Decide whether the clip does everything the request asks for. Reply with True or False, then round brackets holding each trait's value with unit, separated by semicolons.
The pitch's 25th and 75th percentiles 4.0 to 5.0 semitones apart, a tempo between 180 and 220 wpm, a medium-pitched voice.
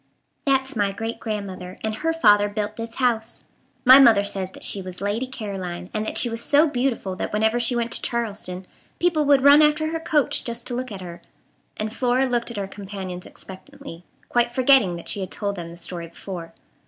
False (4.7 semitones; 205 wpm; 220 Hz)